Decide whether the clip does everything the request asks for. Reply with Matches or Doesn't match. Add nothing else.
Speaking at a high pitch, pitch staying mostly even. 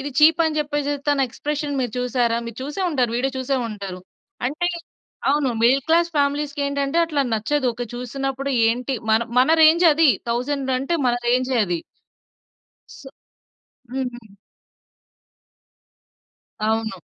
Doesn't match